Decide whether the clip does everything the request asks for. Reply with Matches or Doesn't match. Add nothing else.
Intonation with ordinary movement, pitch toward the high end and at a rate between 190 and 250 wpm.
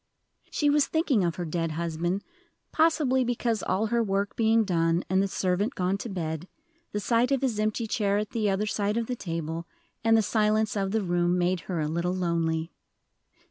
Matches